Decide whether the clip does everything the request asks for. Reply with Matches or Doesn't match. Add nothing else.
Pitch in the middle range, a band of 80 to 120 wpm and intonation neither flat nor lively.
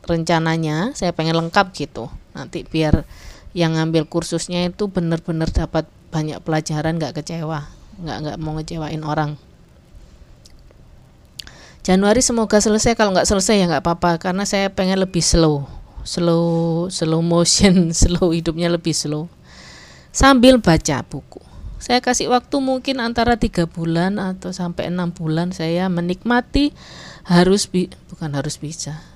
Doesn't match